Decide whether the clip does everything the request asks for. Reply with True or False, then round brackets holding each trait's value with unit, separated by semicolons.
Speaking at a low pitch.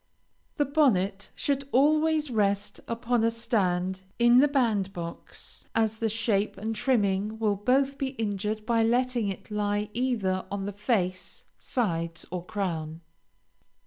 False (215 Hz)